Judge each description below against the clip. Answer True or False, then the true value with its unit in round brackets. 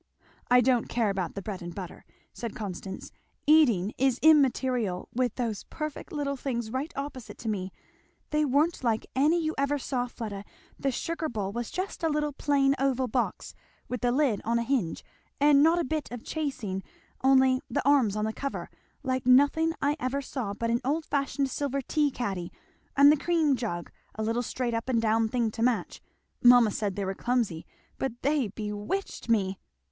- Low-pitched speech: False (250 Hz)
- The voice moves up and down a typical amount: True (4.4 semitones)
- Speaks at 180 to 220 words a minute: True (185 wpm)